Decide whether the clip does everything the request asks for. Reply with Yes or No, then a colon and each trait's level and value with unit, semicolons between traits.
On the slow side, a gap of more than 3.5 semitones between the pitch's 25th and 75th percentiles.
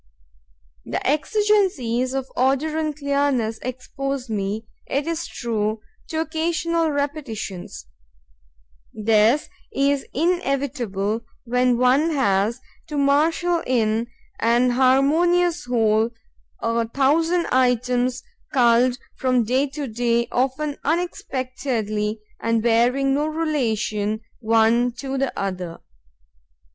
Yes: slow, 100 wpm; average, 4.2 semitones